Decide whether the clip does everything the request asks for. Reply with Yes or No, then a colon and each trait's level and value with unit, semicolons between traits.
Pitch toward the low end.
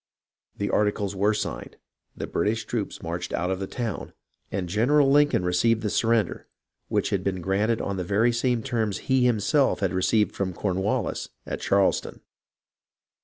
Yes: low, 105 Hz